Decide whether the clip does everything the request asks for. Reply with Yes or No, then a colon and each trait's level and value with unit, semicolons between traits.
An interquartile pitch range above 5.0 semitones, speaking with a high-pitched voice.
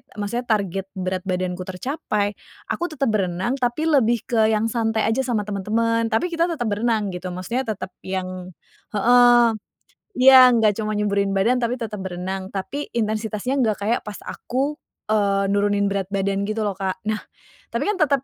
No: average, 3.6 semitones; high, 215 Hz